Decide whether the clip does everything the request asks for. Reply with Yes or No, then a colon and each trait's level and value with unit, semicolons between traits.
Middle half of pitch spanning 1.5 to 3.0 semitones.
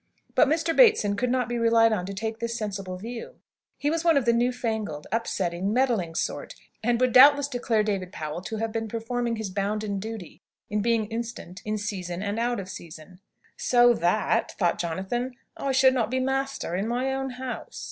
No: average, 4.0 semitones